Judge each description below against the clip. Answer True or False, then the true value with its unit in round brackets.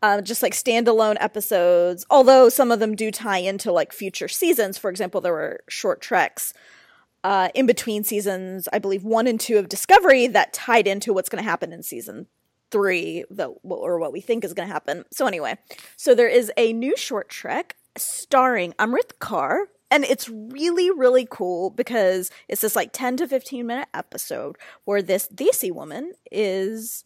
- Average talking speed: True (180 wpm)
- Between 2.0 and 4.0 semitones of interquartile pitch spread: False (5.0 semitones)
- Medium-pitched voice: False (225 Hz)